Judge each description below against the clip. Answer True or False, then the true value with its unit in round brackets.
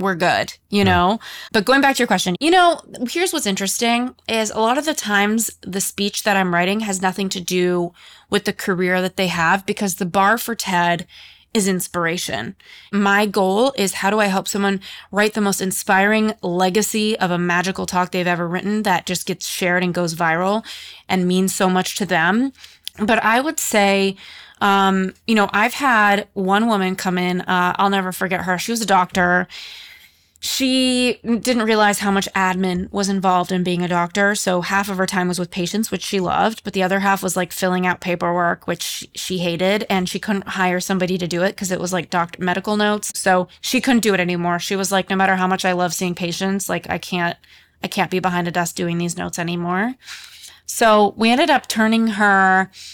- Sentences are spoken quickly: True (210 wpm)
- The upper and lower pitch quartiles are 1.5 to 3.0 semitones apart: True (2.5 semitones)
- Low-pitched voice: False (190 Hz)